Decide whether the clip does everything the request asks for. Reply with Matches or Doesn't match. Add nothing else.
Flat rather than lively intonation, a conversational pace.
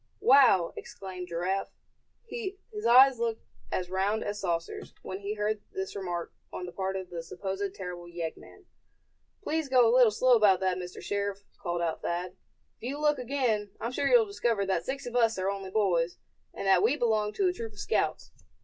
Doesn't match